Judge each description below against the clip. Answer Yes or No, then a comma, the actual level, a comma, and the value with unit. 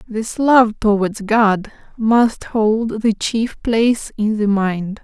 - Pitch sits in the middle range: No, high, 220 Hz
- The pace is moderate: Yes, average, 145 wpm